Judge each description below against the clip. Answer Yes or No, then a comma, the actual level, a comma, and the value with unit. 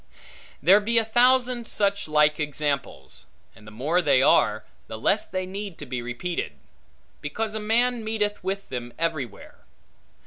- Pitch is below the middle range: No, medium, 180 Hz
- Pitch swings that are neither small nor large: No, wide, 7.4 semitones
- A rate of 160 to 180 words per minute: No, average, 150 wpm